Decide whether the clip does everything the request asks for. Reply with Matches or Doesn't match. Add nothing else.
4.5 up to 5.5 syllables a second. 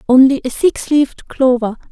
Matches